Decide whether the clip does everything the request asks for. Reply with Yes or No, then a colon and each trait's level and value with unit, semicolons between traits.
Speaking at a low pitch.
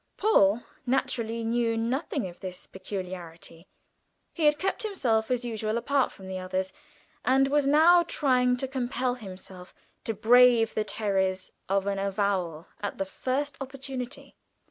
No: high, 230 Hz